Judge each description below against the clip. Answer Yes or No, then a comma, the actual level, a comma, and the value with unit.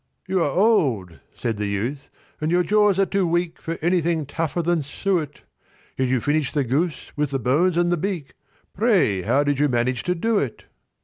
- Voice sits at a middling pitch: Yes, medium, 155 Hz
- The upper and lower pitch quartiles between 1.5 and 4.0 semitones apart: No, average, 5.0 semitones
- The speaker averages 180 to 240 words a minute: Yes, average, 195 wpm